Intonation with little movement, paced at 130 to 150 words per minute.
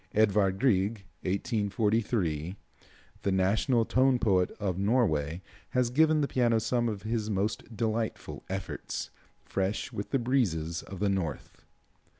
No: average, 3.7 semitones; slow, 135 wpm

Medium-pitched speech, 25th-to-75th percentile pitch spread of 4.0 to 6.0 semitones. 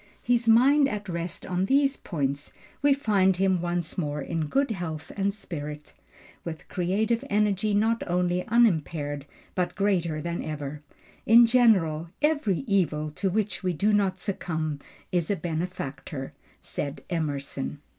Yes: medium, 180 Hz; average, 5.2 semitones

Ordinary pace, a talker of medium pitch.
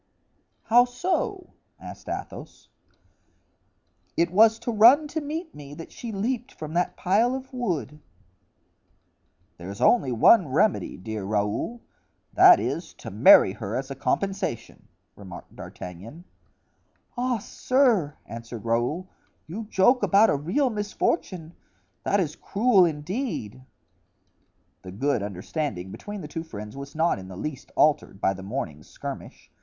No: slow, 130 wpm; medium, 170 Hz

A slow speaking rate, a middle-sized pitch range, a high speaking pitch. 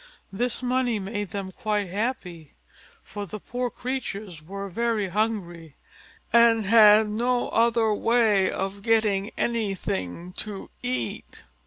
Yes: slow, 120 wpm; average, 3.3 semitones; high, 210 Hz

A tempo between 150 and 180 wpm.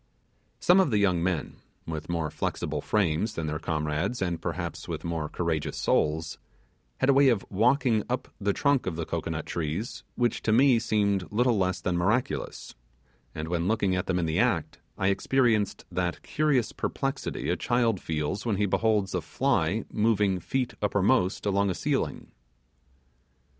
Yes: average, 165 wpm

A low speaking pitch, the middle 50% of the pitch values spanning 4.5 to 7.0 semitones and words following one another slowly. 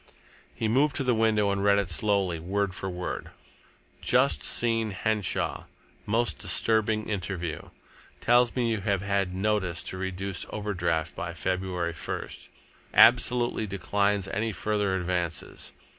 No: low, 100 Hz; average, 3.1 semitones; slow, 130 wpm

